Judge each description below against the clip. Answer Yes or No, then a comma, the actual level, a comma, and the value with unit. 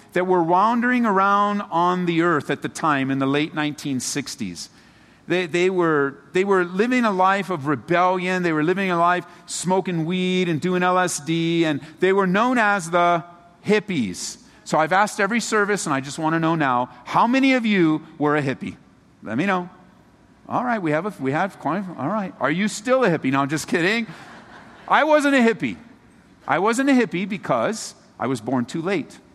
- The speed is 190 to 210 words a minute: Yes, average, 200 wpm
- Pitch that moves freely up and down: No, average, 4.6 semitones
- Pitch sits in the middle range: Yes, medium, 180 Hz